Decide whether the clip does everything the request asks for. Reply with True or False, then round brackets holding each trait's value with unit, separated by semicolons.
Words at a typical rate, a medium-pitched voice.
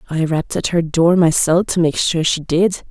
False (230 wpm; 165 Hz)